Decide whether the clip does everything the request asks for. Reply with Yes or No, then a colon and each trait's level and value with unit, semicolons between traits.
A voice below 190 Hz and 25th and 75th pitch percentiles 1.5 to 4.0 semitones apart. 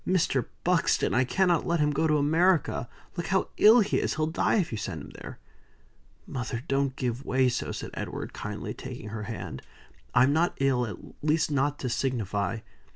No: medium, 140 Hz; average, 5.0 semitones